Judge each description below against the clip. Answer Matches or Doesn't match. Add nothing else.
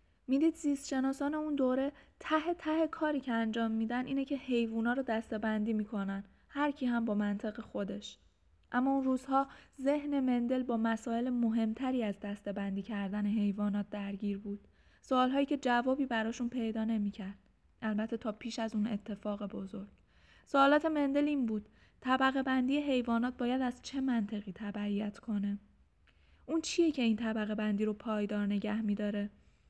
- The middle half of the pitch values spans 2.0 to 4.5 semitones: Matches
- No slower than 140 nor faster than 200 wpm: Matches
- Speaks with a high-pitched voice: Matches